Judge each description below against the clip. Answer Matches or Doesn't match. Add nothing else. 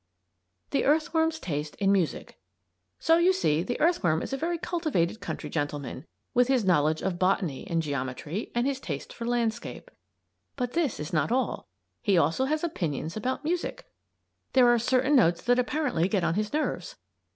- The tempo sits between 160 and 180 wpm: Matches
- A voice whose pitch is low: Doesn't match